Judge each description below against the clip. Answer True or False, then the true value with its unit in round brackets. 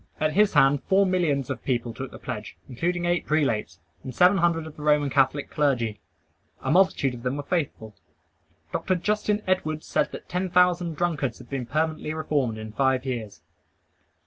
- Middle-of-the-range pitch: True (150 Hz)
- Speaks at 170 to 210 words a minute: True (175 wpm)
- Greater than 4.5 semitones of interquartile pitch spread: True (5.1 semitones)